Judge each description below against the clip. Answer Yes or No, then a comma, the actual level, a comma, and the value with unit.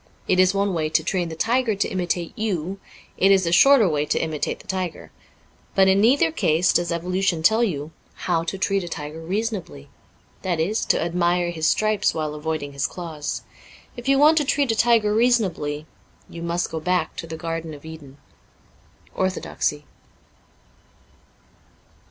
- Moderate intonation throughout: Yes, average, 3.9 semitones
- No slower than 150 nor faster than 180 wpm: Yes, average, 175 wpm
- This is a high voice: No, medium, 175 Hz